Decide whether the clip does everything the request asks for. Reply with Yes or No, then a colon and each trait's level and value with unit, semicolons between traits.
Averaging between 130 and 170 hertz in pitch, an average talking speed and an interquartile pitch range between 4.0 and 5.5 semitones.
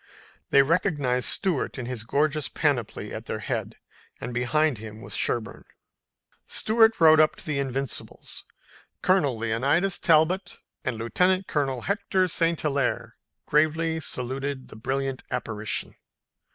No: medium, 140 Hz; slow, 125 wpm; average, 4.7 semitones